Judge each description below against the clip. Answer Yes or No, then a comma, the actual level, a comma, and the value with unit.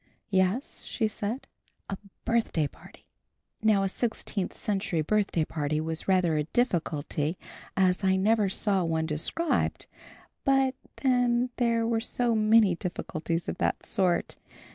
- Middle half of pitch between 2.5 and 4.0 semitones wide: No, wide, 5.5 semitones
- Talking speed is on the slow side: Yes, slow, 130 wpm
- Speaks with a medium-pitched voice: No, high, 195 Hz